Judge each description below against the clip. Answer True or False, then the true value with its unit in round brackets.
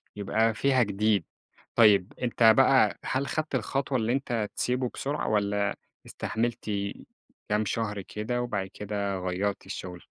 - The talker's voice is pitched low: True (110 Hz)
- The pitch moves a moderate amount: True (3.4 semitones)